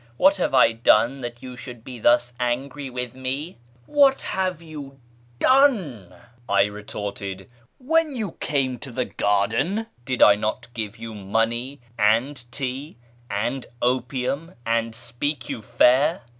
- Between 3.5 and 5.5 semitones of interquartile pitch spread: Yes, average, 3.9 semitones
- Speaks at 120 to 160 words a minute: Yes, average, 155 wpm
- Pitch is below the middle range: Yes, low, 125 Hz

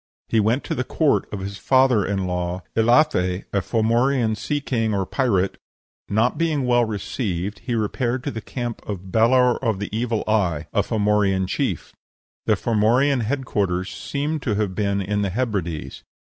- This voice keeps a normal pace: Yes, average, 170 wpm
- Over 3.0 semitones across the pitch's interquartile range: Yes, average, 4.1 semitones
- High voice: No, low, 110 Hz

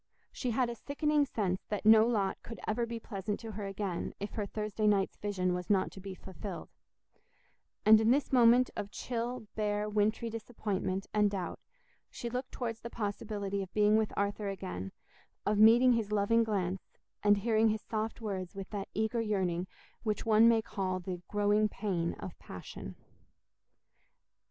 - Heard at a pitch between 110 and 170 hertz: No, high, 210 Hz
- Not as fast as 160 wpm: No, average, 170 wpm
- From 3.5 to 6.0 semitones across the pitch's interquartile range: No, narrow, 2.5 semitones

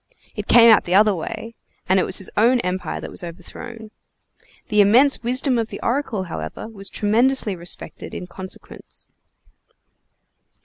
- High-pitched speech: Yes, high, 210 Hz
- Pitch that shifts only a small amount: No, average, 3.8 semitones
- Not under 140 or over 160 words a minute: Yes, average, 150 wpm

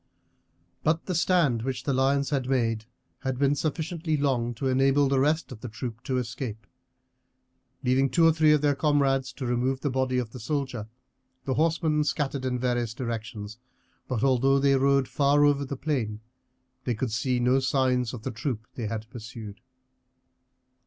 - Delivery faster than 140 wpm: Yes, average, 175 wpm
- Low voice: Yes, low, 130 Hz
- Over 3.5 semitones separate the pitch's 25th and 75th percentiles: No, average, 2.8 semitones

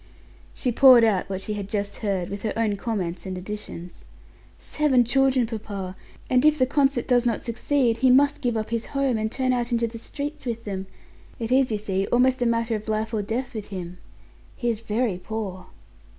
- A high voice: Yes, high, 230 Hz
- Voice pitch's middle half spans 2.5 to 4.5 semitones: Yes, average, 3.7 semitones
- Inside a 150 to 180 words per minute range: No, fast, 205 wpm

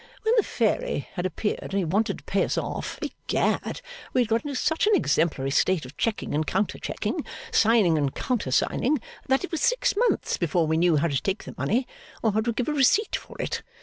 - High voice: Yes, high, 220 Hz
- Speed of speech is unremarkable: No, fast, 220 wpm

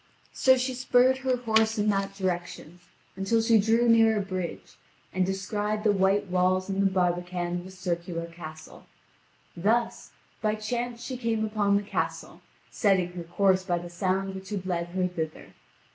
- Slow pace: No, average, 170 wpm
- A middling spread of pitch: Yes, average, 3.6 semitones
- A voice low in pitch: No, high, 195 Hz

